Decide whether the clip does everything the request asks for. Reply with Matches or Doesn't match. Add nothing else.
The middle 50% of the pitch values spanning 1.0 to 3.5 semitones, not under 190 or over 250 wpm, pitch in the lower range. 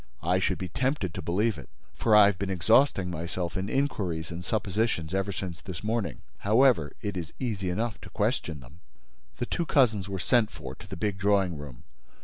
Doesn't match